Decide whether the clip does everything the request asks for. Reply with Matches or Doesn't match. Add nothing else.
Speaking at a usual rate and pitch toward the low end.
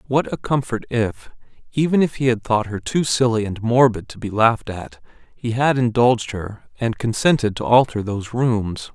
Matches